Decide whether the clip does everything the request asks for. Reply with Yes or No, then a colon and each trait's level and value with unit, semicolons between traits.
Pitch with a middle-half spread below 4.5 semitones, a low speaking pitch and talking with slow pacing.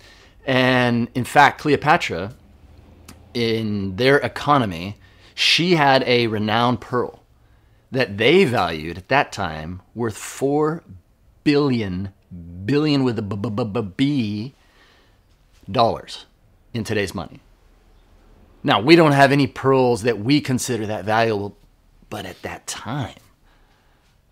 No: average, 5.1 semitones; low, 110 Hz; slow, 120 wpm